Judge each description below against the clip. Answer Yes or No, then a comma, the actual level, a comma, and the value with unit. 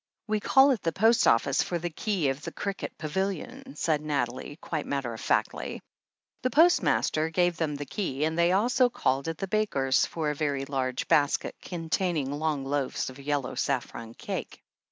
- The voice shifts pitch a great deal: Yes, wide, 5.8 semitones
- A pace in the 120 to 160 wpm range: No, average, 175 wpm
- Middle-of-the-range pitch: Yes, medium, 155 Hz